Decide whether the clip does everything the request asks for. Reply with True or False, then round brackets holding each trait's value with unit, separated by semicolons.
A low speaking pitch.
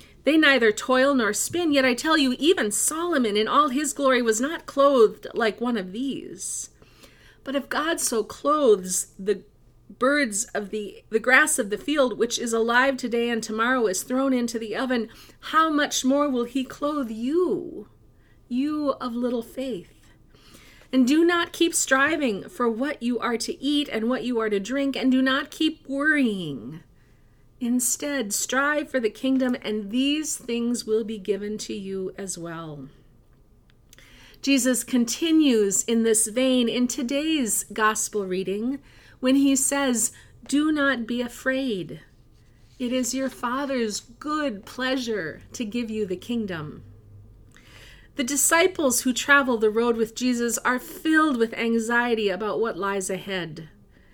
False (245 Hz)